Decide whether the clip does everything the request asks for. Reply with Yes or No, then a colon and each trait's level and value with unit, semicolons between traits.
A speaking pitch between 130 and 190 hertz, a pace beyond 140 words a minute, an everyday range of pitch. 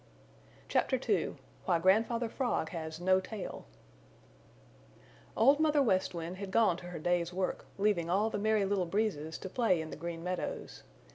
Yes: medium, 185 Hz; average, 160 wpm; average, 4.2 semitones